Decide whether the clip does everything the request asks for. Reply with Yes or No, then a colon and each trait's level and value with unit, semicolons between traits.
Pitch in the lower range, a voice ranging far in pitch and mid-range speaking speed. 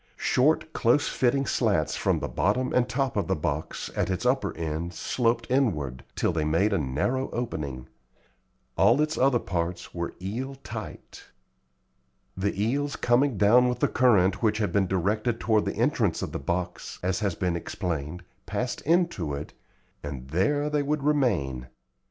Yes: low, 105 Hz; wide, 6.9 semitones; average, 165 wpm